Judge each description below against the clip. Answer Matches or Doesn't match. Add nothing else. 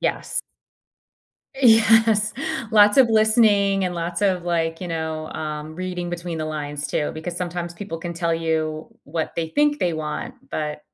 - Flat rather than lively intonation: Doesn't match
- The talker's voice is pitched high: Doesn't match